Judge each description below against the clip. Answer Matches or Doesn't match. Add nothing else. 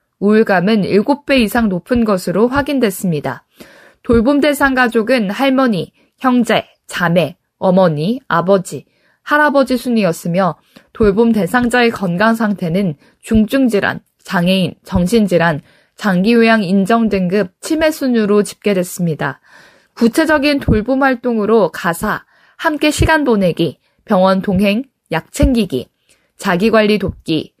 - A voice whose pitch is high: Matches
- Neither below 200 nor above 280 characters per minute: Matches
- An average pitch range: Matches